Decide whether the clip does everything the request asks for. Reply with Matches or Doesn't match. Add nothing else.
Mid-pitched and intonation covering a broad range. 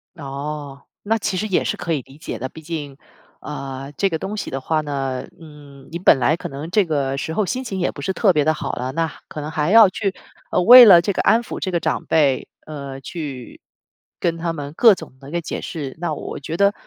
Doesn't match